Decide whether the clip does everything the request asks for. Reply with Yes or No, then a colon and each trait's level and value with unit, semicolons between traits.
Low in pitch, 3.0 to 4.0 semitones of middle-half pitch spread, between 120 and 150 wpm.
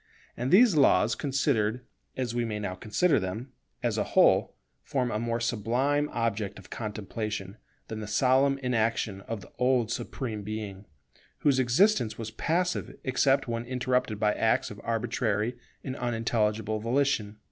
Yes: low, 115 Hz; average, 3.4 semitones; average, 145 wpm